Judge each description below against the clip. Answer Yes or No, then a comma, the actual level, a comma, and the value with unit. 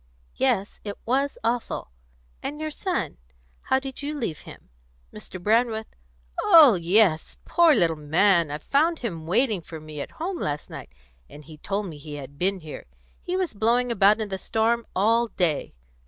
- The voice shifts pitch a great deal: Yes, wide, 7.4 semitones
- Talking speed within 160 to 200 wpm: Yes, average, 175 wpm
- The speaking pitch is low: No, high, 210 Hz